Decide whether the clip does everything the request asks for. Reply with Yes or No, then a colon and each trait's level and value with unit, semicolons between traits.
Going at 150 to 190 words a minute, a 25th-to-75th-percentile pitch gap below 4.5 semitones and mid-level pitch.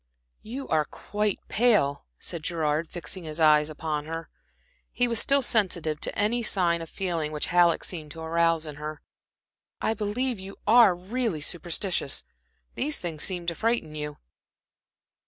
No: average, 155 wpm; average, 5.3 semitones; medium, 170 Hz